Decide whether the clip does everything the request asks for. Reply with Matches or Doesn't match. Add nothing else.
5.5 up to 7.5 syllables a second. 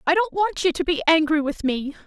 Matches